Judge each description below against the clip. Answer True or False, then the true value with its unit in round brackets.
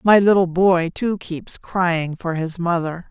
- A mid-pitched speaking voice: True (175 Hz)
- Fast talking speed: False (175 wpm)